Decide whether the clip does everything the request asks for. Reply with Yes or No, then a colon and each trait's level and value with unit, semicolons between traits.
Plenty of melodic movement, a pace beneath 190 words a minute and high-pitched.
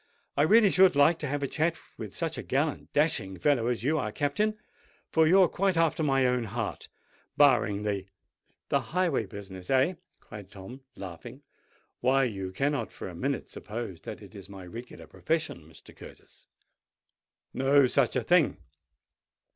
No: wide, 7.1 semitones; average, 155 wpm; low, 130 Hz